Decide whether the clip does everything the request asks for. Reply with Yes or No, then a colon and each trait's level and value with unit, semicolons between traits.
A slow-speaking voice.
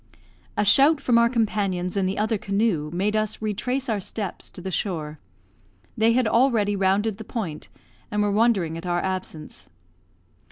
No: average, 165 wpm